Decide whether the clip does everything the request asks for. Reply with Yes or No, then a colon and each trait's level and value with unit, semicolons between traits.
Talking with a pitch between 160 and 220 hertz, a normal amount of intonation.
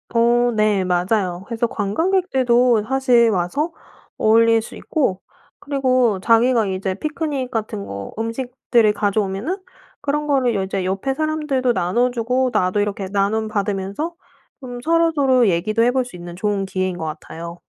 No: high, 230 Hz; average, 4.9 semitones